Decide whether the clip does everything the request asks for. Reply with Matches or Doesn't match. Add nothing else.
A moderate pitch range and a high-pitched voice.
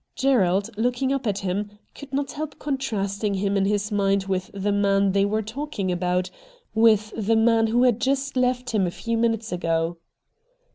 Matches